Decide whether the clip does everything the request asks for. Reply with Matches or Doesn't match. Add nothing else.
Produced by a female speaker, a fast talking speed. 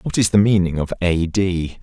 Doesn't match